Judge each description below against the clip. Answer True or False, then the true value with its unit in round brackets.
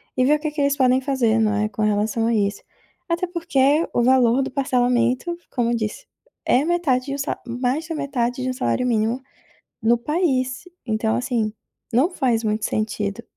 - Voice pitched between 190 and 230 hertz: False (250 Hz)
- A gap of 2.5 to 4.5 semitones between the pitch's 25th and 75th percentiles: True (3.8 semitones)